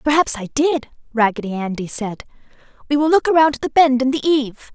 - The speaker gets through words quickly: No, average, 190 wpm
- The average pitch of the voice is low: No, very high, 265 Hz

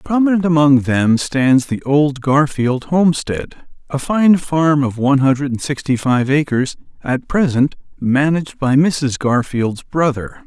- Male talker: Yes, male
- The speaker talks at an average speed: Yes, average, 145 wpm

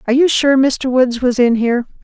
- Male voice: No, female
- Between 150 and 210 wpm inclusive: No, fast, 235 wpm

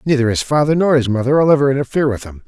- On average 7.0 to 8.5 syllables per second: Yes, 7.7 syllables/s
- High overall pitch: No, low, 135 Hz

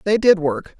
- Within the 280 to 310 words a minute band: No, fast, 225 wpm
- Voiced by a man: No, female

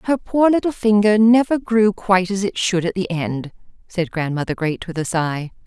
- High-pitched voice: Yes, high, 200 Hz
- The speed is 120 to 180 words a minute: No, average, 200 wpm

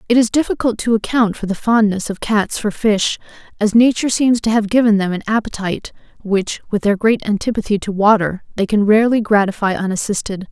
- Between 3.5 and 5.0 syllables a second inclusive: No, 5.7 syllables/s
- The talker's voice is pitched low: No, high, 210 Hz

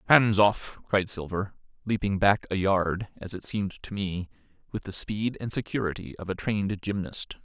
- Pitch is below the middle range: Yes, low, 100 Hz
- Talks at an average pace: Yes, average, 175 wpm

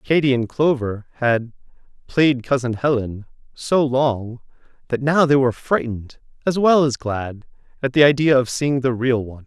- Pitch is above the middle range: No, low, 130 Hz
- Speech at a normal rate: Yes, average, 165 wpm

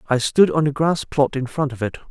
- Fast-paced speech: Yes, fast, 285 wpm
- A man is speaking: Yes, male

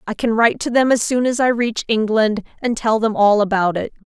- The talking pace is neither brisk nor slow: No, fast, 250 wpm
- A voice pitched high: Yes, high, 225 Hz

